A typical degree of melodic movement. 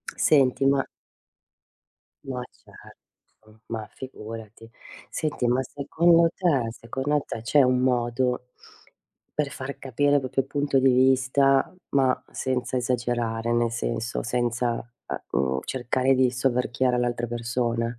No: narrow, 2.3 semitones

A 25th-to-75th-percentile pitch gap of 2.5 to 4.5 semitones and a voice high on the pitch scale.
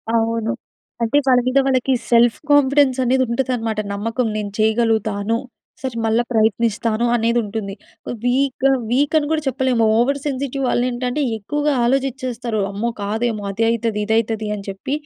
Yes: average, 3.0 semitones; high, 235 Hz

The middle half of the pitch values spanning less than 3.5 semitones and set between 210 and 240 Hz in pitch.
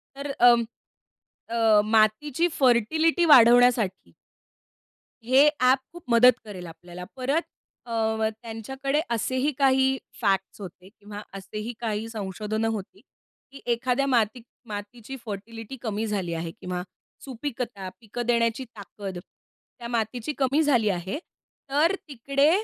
No: average, 4.1 semitones; high, 230 Hz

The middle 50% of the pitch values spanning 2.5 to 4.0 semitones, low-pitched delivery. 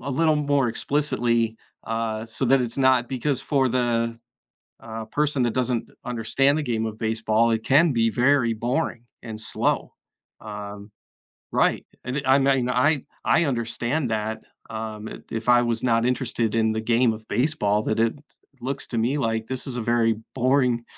Yes: average, 2.8 semitones; low, 120 Hz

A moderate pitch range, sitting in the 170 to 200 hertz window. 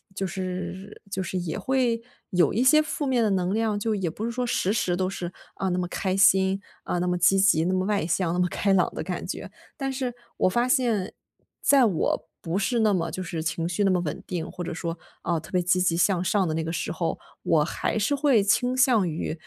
Yes: average, 3.8 semitones; high, 190 Hz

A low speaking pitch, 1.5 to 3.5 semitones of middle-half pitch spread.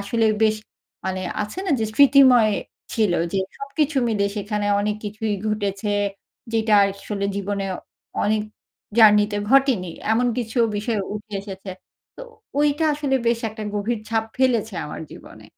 No: high, 215 Hz; average, 2.8 semitones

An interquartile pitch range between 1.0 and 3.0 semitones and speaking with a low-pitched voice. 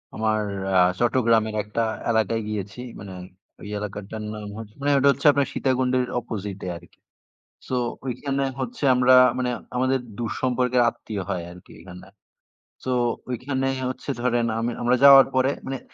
No: average, 3.5 semitones; low, 120 Hz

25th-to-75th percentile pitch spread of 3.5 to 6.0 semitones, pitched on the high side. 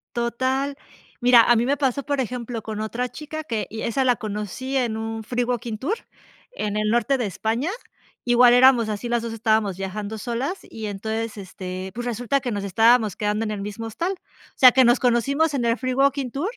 No: average, 3.1 semitones; high, 235 Hz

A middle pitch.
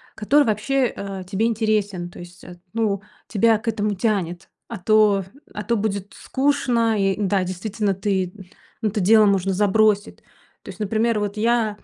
No: high, 210 Hz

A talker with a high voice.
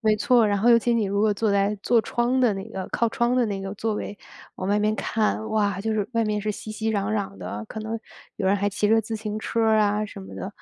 Yes: high, 215 Hz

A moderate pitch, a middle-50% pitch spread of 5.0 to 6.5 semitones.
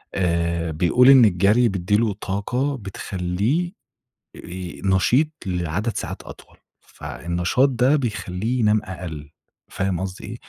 No: low, 100 Hz; average, 5.3 semitones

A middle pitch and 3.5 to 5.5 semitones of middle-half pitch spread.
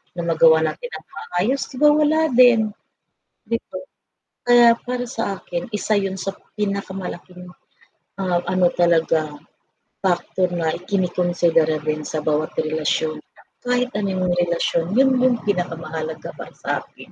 Yes: medium, 180 Hz; average, 4.7 semitones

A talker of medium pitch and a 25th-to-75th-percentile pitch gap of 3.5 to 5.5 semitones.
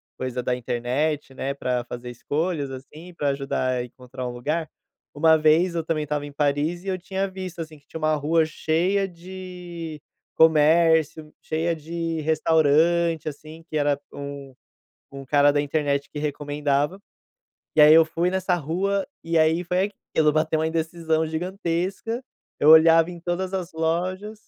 No: medium, 160 Hz; average, 2.8 semitones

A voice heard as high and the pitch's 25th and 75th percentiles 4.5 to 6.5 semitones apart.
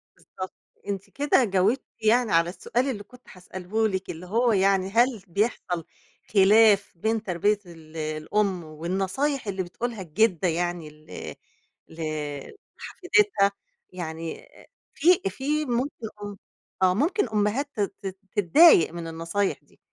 Yes: high, 200 Hz; average, 4.9 semitones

